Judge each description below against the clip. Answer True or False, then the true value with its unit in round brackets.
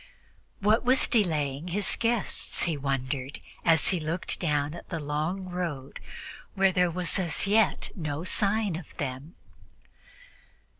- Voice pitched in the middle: True (170 Hz)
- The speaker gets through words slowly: True (130 wpm)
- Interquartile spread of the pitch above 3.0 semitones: True (4.6 semitones)